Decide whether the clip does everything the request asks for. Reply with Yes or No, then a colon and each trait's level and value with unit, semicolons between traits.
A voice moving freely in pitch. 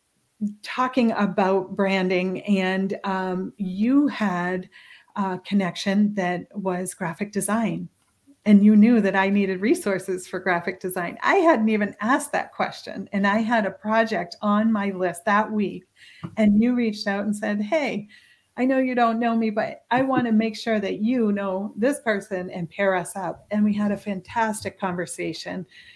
No: average, 2.7 semitones